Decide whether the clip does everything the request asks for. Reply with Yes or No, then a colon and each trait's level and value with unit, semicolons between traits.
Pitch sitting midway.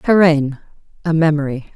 Yes: medium, 155 Hz